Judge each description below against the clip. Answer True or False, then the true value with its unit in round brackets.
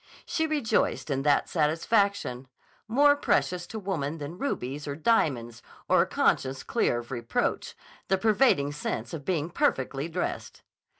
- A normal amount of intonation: False (6.9 semitones)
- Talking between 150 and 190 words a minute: False (140 wpm)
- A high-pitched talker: False (155 Hz)